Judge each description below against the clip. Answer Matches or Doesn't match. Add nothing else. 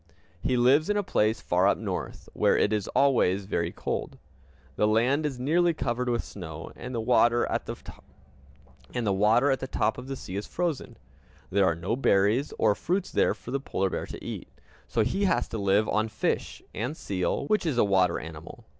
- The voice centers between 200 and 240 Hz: Doesn't match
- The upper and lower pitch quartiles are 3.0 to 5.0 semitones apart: Doesn't match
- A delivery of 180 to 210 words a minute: Matches